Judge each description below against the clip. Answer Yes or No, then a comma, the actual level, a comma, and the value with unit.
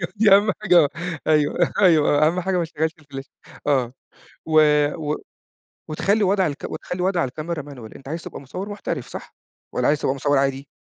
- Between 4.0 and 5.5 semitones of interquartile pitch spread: Yes, average, 4.3 semitones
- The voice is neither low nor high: Yes, medium, 155 Hz